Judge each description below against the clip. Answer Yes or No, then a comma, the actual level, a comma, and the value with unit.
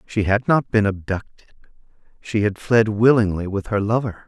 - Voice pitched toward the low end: Yes, low, 105 Hz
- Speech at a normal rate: Yes, average, 155 wpm